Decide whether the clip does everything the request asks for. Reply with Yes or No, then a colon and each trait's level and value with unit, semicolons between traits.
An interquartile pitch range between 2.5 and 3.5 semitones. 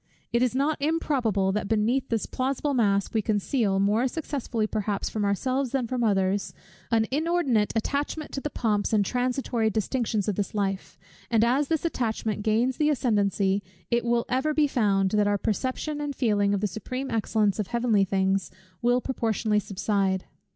No: average, 4.2 semitones